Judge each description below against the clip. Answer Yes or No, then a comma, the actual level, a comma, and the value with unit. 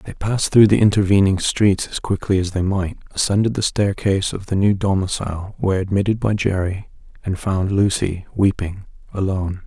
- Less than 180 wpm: Yes, average, 170 wpm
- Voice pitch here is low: Yes, very low, 95 Hz